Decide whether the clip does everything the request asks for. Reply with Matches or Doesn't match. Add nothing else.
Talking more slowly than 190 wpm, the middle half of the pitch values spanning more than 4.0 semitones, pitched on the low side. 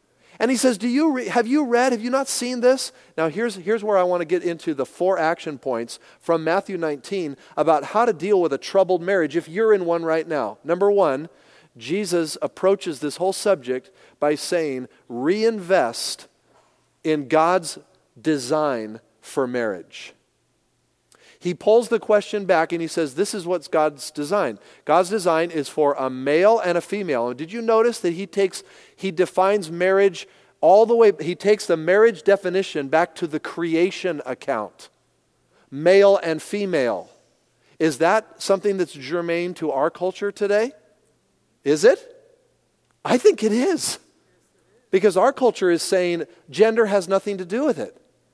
Doesn't match